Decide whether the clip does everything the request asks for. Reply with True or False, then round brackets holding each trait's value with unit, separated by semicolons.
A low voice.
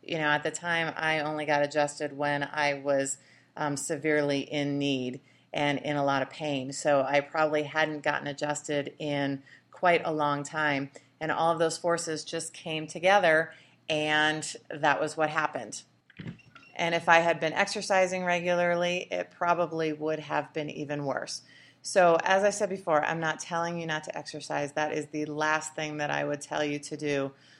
False (150 Hz)